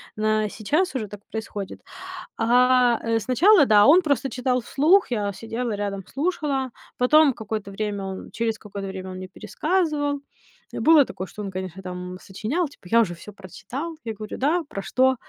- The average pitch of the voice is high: Yes, high, 225 Hz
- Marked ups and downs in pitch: Yes, wide, 5.8 semitones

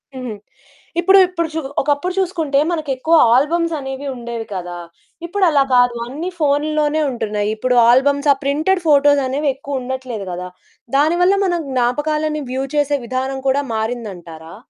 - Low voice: No, very high, 280 Hz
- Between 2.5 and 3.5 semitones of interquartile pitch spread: No, average, 3.9 semitones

